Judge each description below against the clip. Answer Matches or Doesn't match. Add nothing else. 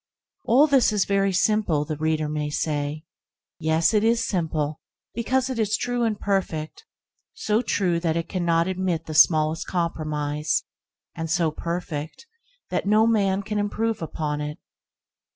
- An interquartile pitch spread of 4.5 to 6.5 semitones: Matches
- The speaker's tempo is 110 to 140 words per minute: Doesn't match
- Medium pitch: Matches